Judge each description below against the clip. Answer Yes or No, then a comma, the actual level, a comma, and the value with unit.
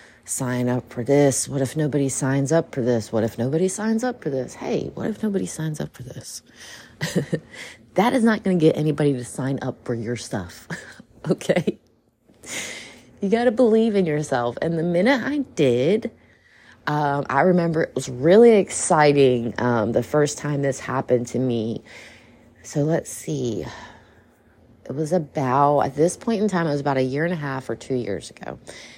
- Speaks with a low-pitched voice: No, medium, 145 Hz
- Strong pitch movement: Yes, wide, 6.0 semitones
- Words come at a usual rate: Yes, average, 185 wpm